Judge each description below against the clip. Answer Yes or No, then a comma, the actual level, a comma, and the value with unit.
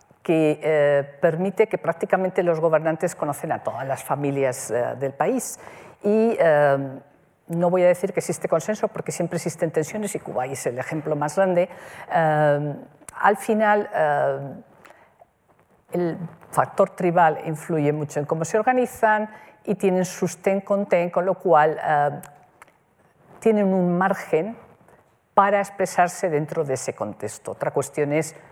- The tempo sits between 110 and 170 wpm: Yes, average, 145 wpm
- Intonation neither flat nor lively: Yes, average, 4.6 semitones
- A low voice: No, medium, 170 Hz